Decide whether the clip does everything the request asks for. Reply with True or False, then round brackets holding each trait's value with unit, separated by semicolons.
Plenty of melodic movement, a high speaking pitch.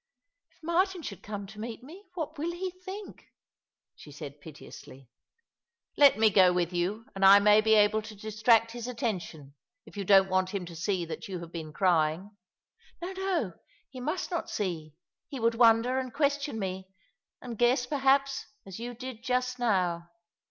True (6.3 semitones; 220 Hz)